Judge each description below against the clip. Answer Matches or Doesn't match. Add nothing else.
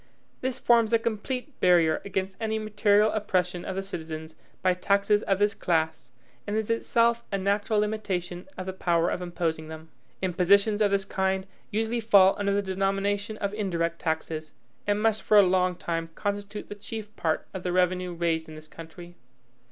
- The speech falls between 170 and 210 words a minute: Matches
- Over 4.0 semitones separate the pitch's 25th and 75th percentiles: Doesn't match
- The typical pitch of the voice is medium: Doesn't match